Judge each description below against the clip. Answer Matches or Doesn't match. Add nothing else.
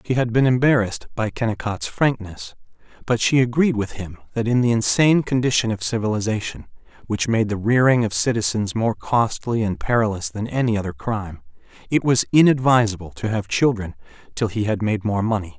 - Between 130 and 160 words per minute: Doesn't match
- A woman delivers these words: Doesn't match